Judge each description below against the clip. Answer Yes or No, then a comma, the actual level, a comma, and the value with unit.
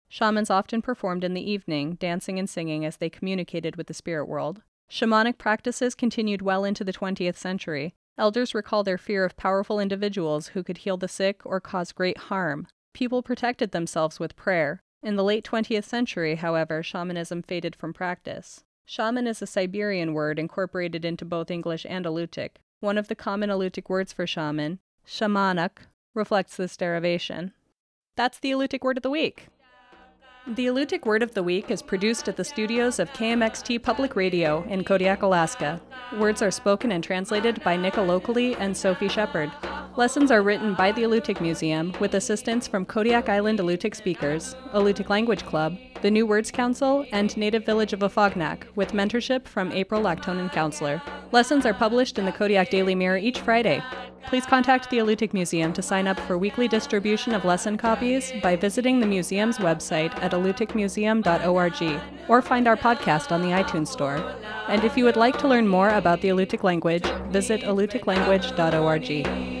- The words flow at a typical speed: Yes, average, 170 wpm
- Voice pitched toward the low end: No, high, 195 Hz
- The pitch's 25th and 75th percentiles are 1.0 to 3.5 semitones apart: No, average, 4.0 semitones